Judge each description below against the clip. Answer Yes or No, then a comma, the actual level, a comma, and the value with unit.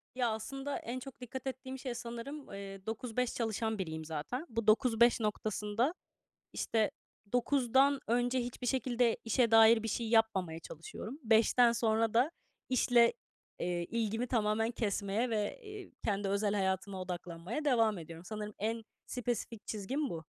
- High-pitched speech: Yes, high, 225 Hz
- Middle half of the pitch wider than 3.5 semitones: No, average, 3.1 semitones